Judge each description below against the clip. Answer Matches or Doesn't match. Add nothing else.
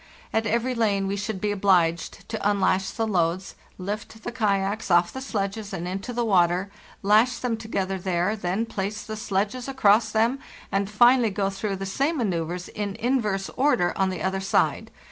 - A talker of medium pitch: Doesn't match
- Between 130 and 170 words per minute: Doesn't match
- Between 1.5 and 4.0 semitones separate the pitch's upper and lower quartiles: Matches